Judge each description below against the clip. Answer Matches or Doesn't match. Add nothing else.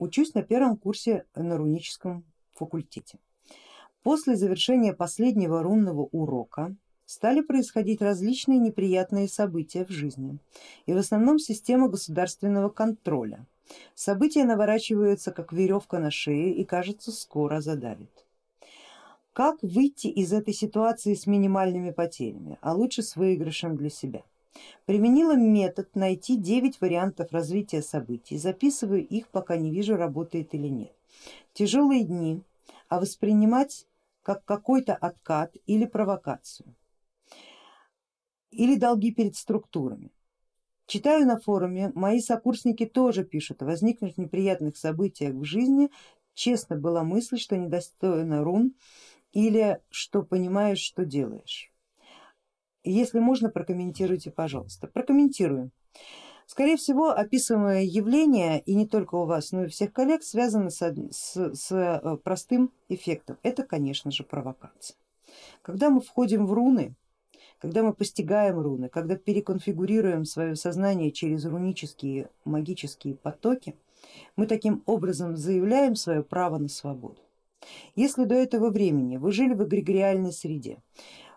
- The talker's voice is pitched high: Matches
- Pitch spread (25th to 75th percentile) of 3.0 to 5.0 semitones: Doesn't match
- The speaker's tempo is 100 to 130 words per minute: Matches